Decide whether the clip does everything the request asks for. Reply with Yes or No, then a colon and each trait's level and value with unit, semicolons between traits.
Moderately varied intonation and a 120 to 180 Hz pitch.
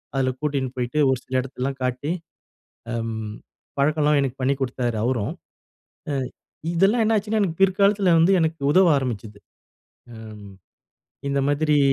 Yes: average, 4.8 semitones; medium, 140 Hz